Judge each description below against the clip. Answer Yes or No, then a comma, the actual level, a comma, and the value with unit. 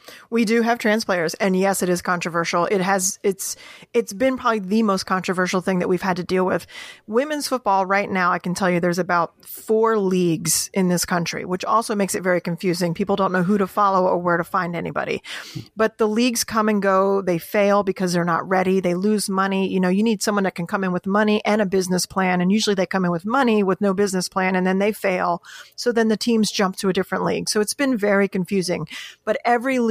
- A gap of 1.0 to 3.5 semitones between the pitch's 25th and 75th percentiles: Yes, average, 2.7 semitones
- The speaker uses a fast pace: Yes, fast, 240 wpm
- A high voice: Yes, high, 195 Hz